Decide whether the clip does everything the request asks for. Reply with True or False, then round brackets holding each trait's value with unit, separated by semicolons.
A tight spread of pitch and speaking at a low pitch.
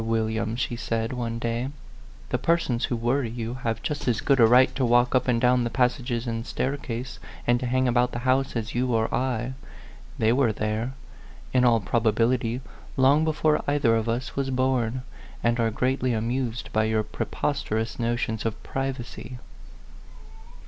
True (2.2 semitones; 120 Hz)